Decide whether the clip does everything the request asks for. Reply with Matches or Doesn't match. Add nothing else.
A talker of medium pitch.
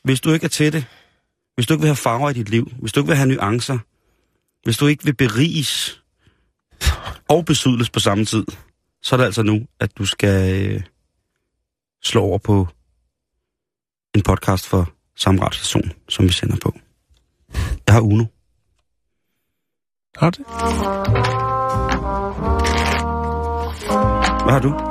Doesn't match